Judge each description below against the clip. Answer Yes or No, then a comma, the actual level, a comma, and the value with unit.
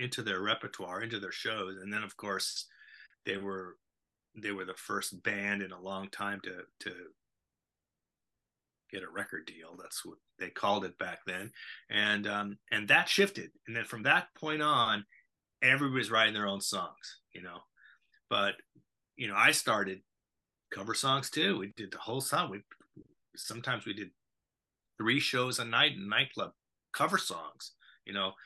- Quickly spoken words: No, average, 165 wpm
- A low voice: Yes, low, 105 Hz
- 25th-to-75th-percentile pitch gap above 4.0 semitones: Yes, average, 4.6 semitones